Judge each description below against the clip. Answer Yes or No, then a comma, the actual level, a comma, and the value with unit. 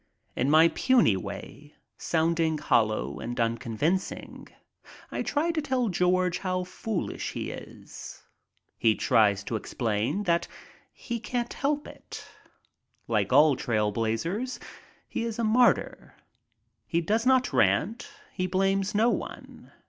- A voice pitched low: No, medium, 170 Hz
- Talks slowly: Yes, slow, 125 wpm